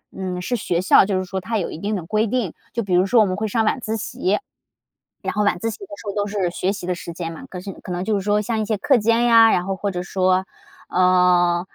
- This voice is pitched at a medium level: No, high, 195 Hz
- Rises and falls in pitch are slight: No, average, 3.0 semitones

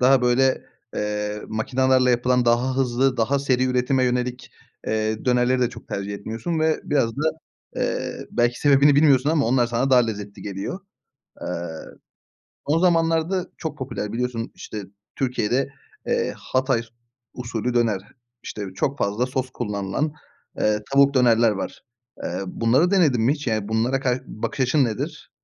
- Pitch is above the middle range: No, low, 125 Hz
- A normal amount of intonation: Yes, average, 3.2 semitones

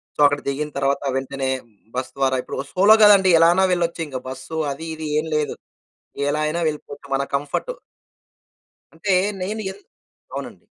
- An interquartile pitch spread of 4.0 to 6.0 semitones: Yes, average, 4.3 semitones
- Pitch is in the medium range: Yes, medium, 150 Hz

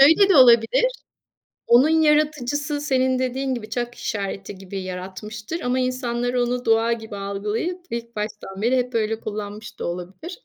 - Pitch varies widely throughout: No, average, 3.8 semitones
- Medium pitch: No, high, 240 Hz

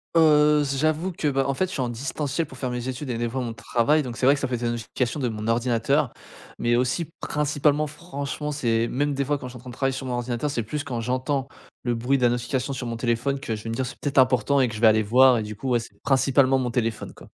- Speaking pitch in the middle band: No, low, 130 Hz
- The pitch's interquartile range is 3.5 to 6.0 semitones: No, average, 3.1 semitones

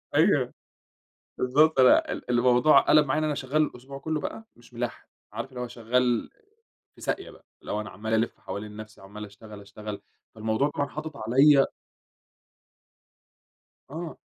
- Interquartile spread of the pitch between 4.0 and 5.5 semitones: Yes, average, 5.1 semitones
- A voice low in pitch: Yes, low, 125 Hz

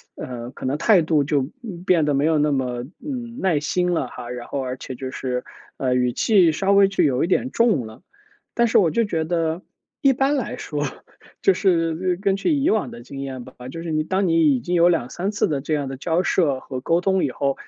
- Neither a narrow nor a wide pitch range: No, wide, 6.0 semitones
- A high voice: No, medium, 160 Hz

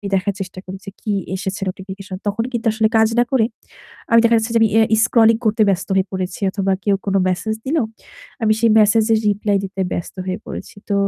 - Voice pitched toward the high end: Yes, high, 205 Hz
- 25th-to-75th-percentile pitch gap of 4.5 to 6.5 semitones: No, narrow, 2.6 semitones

